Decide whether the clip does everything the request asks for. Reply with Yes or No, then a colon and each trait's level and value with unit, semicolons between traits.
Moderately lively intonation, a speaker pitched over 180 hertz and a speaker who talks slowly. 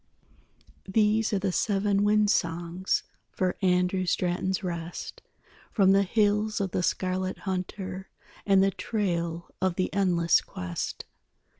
No: narrow, 2.0 semitones; high, 190 Hz; slow, 125 wpm